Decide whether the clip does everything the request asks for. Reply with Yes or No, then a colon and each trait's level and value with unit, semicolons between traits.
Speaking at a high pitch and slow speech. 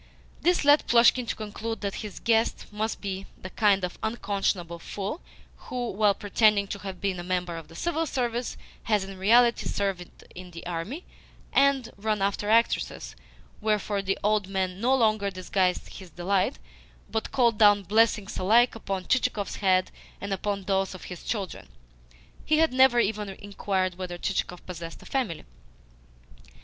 No: high, 200 Hz; average, 160 wpm